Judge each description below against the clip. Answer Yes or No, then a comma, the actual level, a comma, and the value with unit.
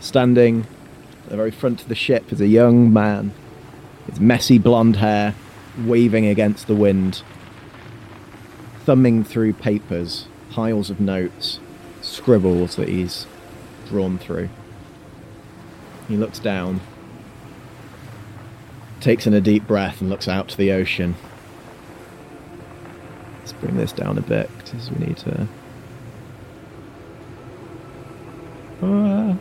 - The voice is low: Yes, low, 110 Hz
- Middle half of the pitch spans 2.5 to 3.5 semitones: Yes, average, 2.9 semitones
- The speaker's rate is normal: No, slow, 115 wpm